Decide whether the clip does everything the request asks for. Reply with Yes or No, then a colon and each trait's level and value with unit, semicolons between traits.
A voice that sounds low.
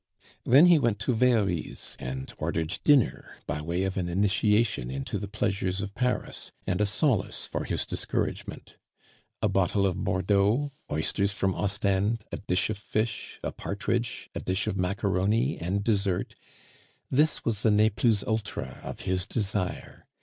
Yes: low, 100 Hz